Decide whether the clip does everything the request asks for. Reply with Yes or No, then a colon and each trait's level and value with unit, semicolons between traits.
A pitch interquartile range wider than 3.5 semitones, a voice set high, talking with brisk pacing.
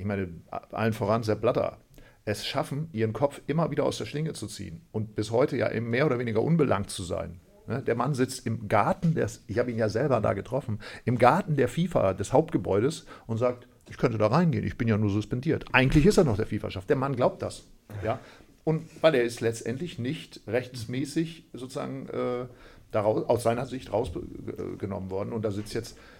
No: average, 4.7 semitones; low, 120 Hz; fast, 195 wpm